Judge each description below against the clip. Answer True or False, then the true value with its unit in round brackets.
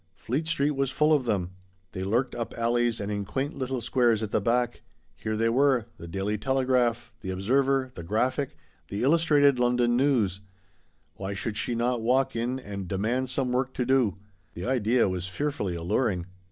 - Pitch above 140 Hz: False (120 Hz)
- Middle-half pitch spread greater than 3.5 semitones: True (4.3 semitones)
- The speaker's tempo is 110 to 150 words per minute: False (175 wpm)